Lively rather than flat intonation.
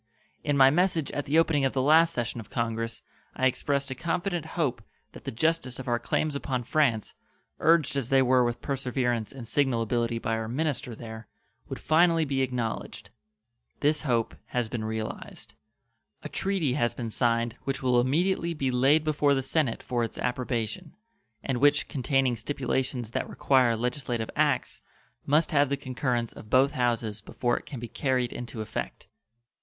No: average, 3.5 semitones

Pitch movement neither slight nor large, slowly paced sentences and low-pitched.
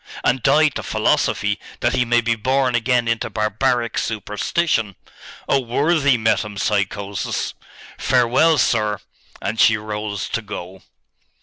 Yes: average, 3.4 semitones; slow, 120 wpm; low, 115 Hz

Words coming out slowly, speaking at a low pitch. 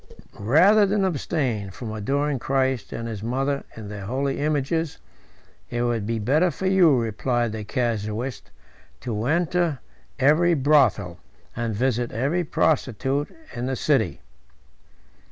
Yes: slow, 130 wpm; low, 130 Hz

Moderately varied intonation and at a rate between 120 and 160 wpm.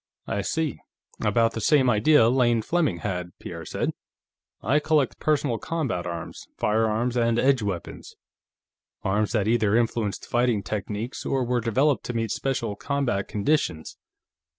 Yes: average, 4.1 semitones; average, 140 wpm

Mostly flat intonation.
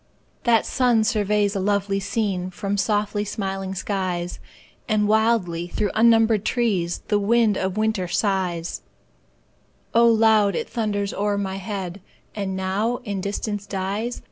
Yes: narrow, 2.3 semitones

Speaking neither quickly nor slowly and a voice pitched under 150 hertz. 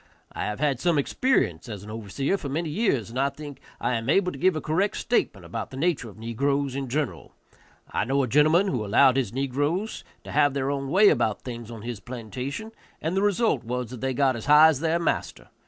No: fast, 225 wpm; low, 135 Hz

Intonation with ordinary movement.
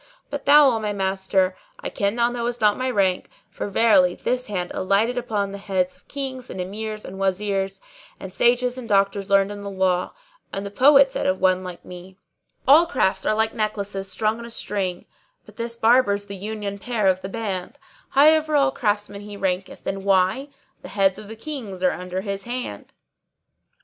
Yes: average, 3.7 semitones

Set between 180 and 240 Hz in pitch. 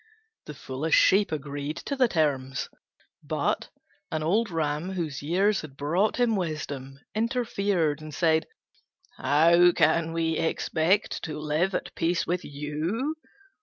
No: medium, 160 Hz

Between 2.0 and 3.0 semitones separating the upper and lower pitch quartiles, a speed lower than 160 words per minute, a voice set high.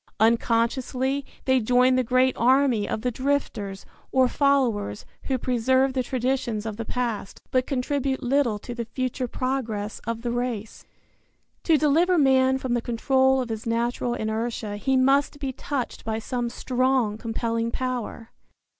Yes: narrow, 2.4 semitones; average, 150 wpm; very high, 250 Hz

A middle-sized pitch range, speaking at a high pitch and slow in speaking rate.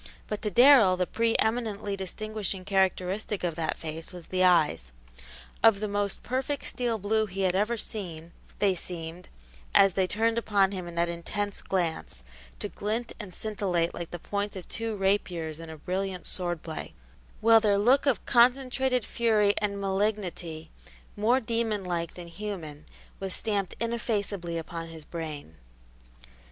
No: average, 3.9 semitones; high, 195 Hz; average, 155 wpm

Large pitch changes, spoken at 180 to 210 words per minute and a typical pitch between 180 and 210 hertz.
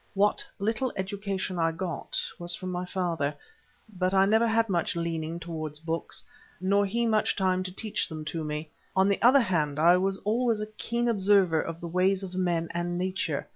No: average, 3.2 semitones; average, 190 wpm; medium, 185 Hz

